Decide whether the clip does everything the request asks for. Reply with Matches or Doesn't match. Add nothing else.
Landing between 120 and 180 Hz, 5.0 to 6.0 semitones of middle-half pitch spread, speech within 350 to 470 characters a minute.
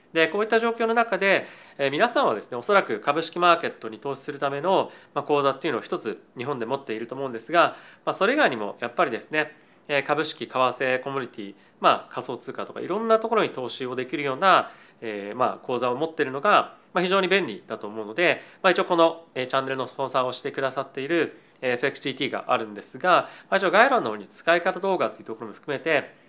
Matches